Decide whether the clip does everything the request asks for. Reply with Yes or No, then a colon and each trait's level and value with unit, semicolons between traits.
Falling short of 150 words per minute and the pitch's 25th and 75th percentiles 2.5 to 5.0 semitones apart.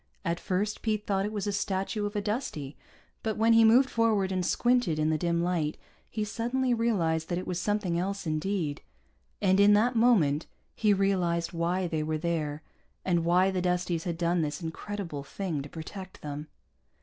No: average, 185 wpm; average, 3.9 semitones